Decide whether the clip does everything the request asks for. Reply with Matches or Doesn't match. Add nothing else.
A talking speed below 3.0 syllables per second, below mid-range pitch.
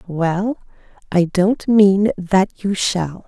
Doesn't match